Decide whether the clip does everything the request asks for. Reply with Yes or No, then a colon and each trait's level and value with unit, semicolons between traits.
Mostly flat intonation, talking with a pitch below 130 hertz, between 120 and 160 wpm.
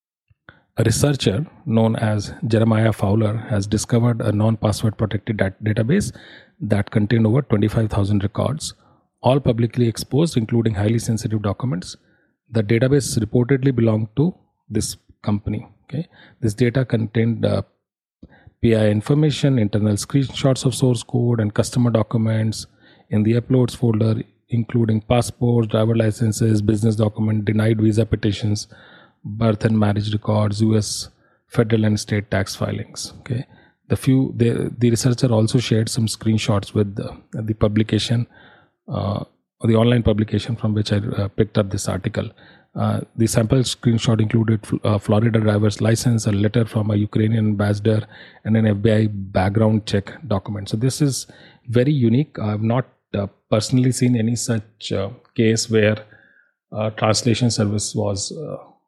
Yes: narrow, 2.0 semitones; low, 110 Hz; average, 140 wpm